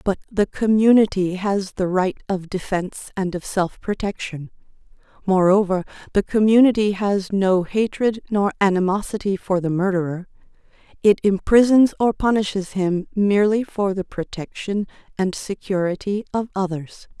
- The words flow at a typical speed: No, slow, 125 wpm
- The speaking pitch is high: Yes, high, 195 Hz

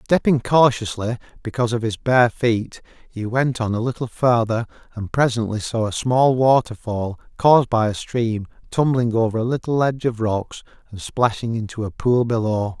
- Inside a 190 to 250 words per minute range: No, average, 170 wpm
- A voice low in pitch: Yes, low, 115 Hz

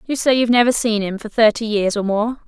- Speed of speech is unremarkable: No, fast, 265 wpm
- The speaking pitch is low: No, high, 225 Hz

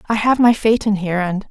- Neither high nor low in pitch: No, high, 210 Hz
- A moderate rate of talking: No, fast, 240 wpm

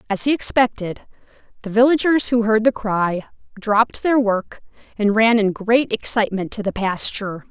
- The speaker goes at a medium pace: Yes, average, 160 wpm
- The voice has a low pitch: No, high, 220 Hz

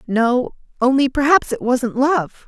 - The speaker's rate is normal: Yes, average, 145 wpm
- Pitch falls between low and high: No, very high, 255 Hz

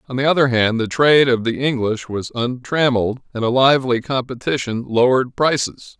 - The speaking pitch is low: Yes, low, 125 Hz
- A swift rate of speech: No, average, 170 wpm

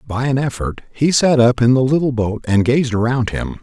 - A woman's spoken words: No, male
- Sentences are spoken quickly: Yes, fast, 230 wpm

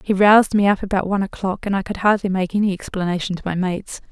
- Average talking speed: No, fast, 250 wpm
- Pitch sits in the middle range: No, high, 195 Hz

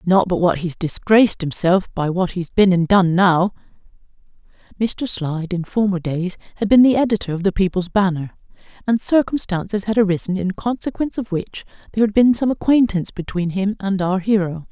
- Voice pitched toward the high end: Yes, high, 195 Hz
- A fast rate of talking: No, average, 180 wpm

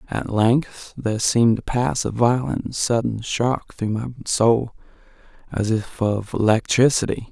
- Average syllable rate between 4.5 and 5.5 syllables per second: No, 4.2 syllables/s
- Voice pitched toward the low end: Yes, low, 115 Hz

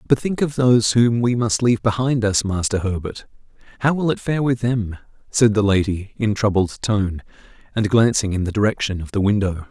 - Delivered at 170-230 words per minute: Yes, average, 200 wpm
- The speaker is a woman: No, male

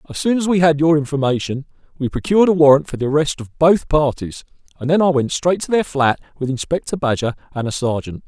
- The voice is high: No, medium, 150 Hz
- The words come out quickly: Yes, fast, 225 wpm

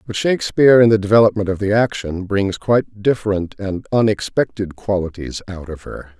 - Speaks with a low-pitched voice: Yes, low, 105 Hz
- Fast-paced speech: No, average, 165 wpm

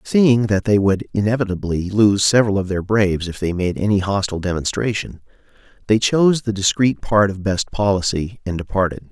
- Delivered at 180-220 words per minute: No, average, 170 wpm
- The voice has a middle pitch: No, low, 100 Hz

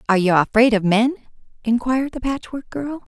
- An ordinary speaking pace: Yes, average, 170 wpm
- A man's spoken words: No, female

